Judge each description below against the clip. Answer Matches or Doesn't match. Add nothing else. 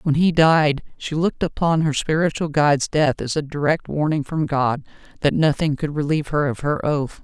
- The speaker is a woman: Matches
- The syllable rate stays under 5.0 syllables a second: Doesn't match